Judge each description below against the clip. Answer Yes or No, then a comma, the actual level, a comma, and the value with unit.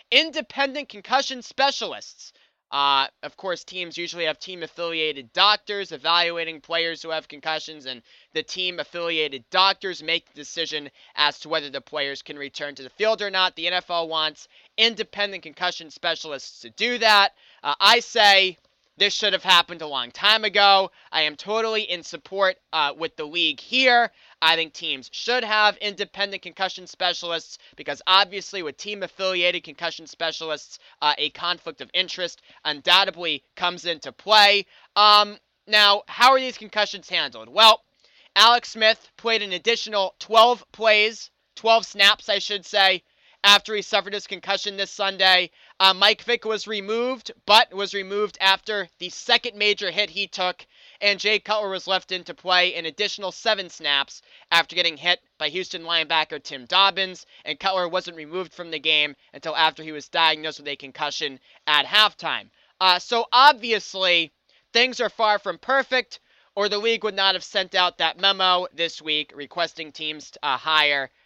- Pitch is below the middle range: No, medium, 185 Hz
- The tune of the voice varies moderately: Yes, average, 4.3 semitones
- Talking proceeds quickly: No, average, 165 wpm